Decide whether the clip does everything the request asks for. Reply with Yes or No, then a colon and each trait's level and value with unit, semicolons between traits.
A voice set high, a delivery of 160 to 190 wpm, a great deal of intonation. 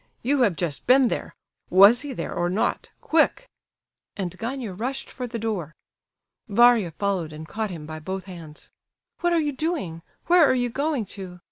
Yes: high, 215 Hz; average, 175 wpm; wide, 6.7 semitones